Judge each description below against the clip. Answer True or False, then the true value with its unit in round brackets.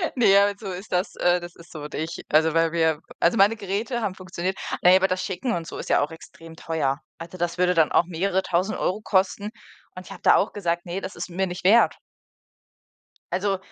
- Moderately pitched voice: True (180 Hz)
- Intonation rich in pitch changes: False (2.6 semitones)